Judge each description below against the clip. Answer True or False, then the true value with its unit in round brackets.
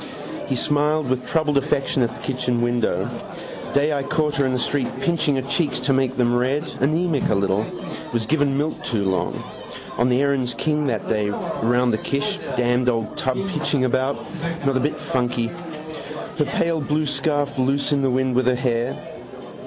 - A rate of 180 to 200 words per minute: True (185 wpm)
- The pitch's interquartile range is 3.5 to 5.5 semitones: False (3.1 semitones)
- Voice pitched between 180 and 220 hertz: False (130 Hz)